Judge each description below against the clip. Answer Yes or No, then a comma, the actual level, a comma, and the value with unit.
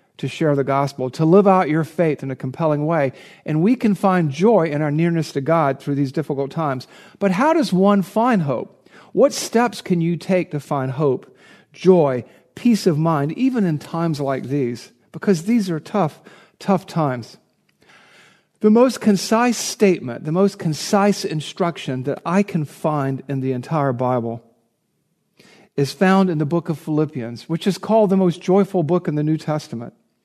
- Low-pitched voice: No, medium, 165 Hz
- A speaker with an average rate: Yes, average, 180 wpm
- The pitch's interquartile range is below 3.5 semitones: No, wide, 5.5 semitones